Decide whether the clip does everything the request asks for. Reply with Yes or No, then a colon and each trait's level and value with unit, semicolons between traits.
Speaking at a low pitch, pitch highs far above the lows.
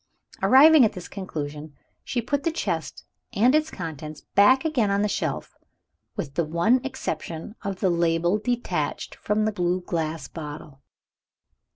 No: medium, 185 Hz; wide, 7.0 semitones